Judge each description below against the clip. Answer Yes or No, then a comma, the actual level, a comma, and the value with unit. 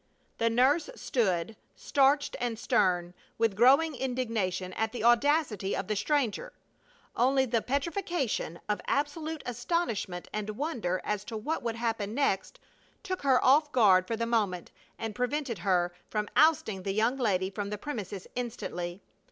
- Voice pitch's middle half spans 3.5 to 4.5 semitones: No, wide, 5.5 semitones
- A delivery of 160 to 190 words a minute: No, average, 150 wpm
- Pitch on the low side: No, high, 230 Hz